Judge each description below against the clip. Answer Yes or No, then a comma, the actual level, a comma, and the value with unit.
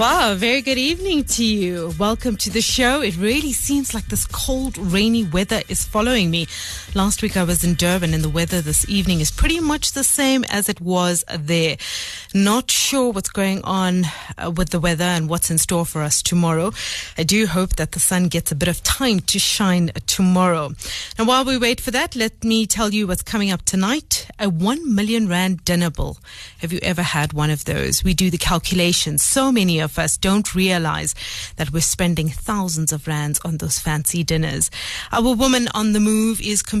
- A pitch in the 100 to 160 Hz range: No, medium, 185 Hz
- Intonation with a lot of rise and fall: No, average, 4.7 semitones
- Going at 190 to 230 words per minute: Yes, average, 200 wpm